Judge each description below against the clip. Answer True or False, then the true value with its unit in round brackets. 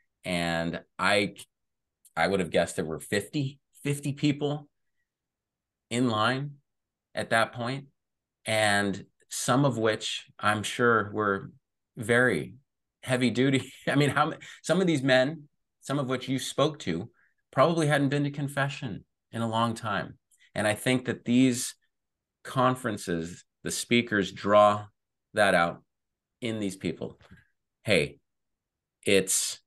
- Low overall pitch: True (120 Hz)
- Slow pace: True (130 wpm)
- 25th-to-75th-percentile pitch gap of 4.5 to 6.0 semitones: True (5.0 semitones)